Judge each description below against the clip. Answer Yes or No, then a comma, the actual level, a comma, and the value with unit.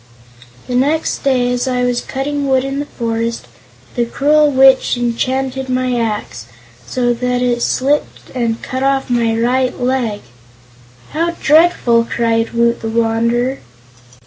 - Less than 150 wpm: Yes, average, 140 wpm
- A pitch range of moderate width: No, narrow, 2.3 semitones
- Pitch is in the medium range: No, very high, 250 Hz